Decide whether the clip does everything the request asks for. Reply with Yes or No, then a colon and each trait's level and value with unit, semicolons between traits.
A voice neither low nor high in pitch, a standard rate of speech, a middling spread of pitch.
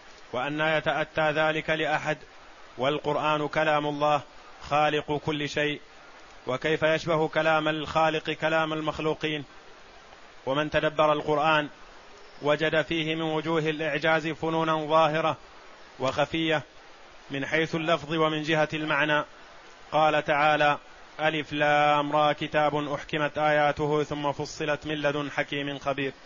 No: medium, 150 Hz; average, 110 wpm; narrow, 1.1 semitones